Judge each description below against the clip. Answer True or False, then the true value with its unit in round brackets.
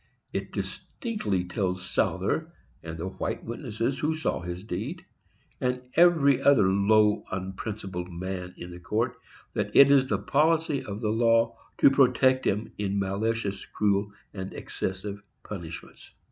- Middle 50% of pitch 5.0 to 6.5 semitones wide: True (5.5 semitones)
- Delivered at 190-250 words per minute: False (140 wpm)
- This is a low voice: True (105 Hz)